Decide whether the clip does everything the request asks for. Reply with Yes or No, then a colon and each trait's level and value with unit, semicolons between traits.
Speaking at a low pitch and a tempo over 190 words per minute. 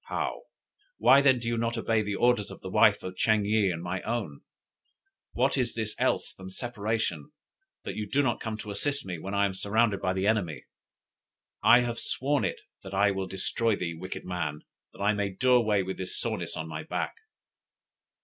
Yes: low, 105 Hz; average, 200 wpm